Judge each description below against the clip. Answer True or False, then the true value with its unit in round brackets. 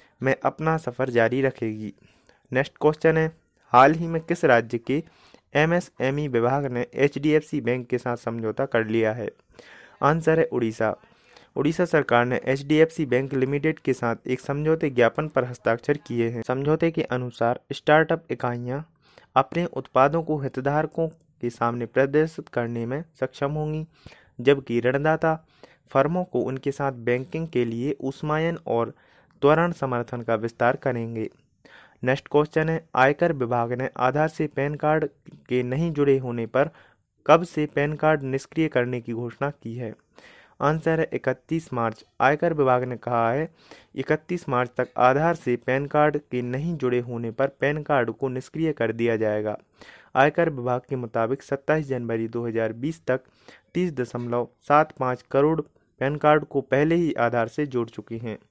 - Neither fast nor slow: True (165 wpm)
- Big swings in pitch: False (4.2 semitones)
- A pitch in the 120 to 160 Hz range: True (135 Hz)